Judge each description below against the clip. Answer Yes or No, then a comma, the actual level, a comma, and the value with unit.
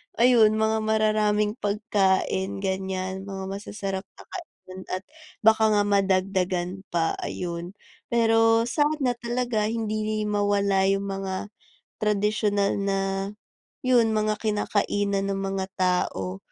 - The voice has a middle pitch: No, high, 205 Hz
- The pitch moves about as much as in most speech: No, narrow, 2.2 semitones